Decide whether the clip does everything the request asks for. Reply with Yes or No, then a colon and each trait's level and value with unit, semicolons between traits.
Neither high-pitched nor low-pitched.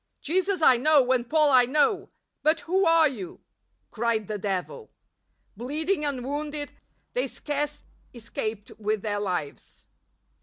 No: very high, 280 Hz